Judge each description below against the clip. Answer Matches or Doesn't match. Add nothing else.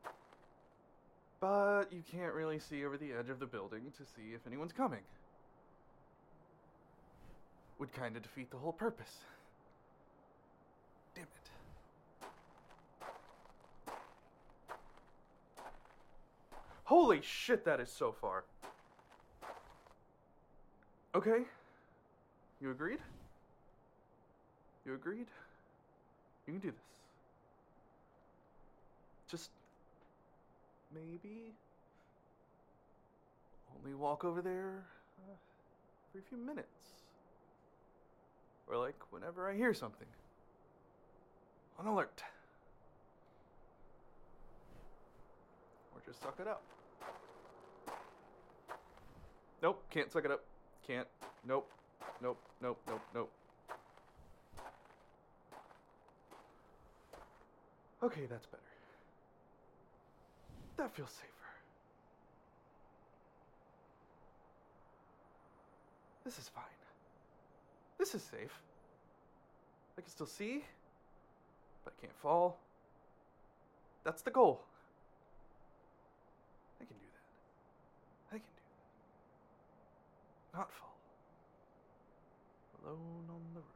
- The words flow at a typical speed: Doesn't match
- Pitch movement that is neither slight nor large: Doesn't match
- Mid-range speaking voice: Matches